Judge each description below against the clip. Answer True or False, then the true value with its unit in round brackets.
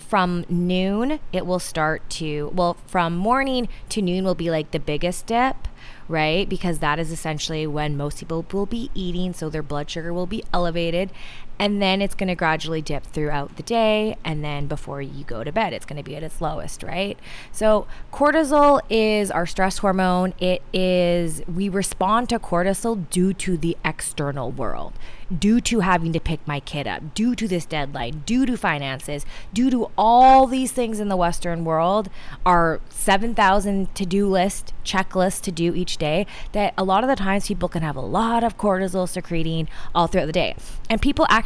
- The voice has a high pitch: False (180 Hz)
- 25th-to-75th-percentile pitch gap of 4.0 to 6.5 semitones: True (4.3 semitones)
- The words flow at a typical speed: True (190 wpm)